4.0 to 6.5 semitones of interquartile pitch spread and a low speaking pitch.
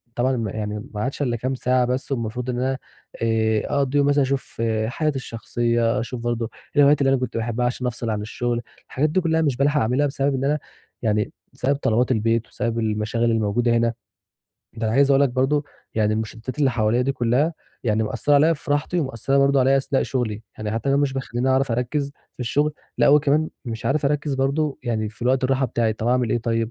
No: average, 3.3 semitones; low, 125 Hz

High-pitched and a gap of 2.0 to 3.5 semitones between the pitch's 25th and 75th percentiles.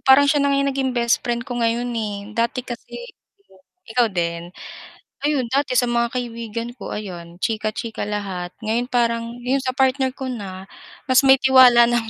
Yes: high, 235 Hz; average, 3.1 semitones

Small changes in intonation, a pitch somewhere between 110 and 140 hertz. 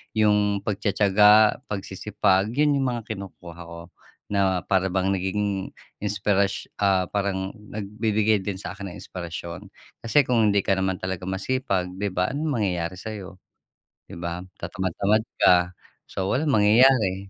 No: narrow, 2.1 semitones; low, 100 Hz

